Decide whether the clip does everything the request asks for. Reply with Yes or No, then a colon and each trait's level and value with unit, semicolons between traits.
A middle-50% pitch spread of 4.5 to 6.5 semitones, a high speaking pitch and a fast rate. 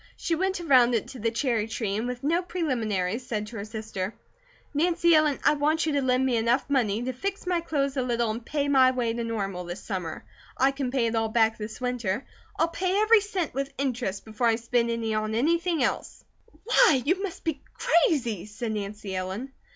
Yes: average, 5.3 semitones; high, 245 Hz; fast, 210 wpm